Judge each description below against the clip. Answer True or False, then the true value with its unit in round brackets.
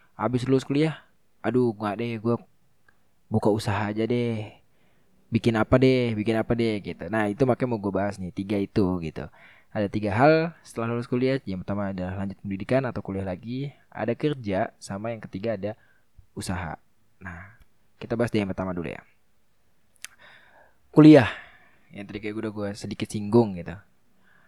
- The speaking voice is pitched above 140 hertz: False (110 Hz)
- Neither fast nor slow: False (165 wpm)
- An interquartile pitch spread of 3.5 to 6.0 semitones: False (3.0 semitones)